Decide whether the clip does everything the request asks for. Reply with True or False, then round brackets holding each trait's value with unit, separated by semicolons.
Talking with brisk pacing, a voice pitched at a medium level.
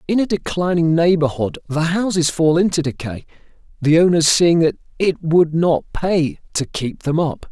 False (170 wpm; 165 Hz)